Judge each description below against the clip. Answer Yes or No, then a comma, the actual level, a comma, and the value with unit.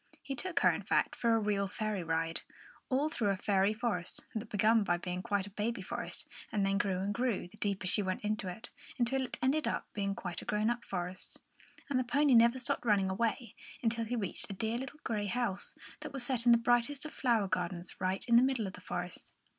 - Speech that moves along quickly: Yes, fast, 230 wpm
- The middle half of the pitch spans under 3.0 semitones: No, average, 3.8 semitones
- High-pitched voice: Yes, high, 215 Hz